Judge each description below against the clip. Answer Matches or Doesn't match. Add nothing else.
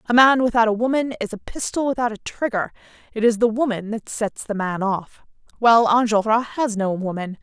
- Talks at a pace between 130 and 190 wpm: Doesn't match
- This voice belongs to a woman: Matches